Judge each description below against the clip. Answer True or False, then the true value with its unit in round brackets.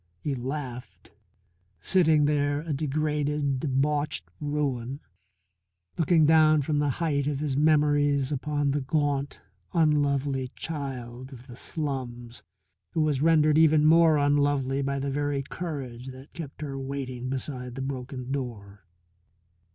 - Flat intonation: True (2.3 semitones)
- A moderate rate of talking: False (130 wpm)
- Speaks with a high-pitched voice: False (140 Hz)